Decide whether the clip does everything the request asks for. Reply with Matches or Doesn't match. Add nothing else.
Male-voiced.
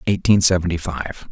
Matches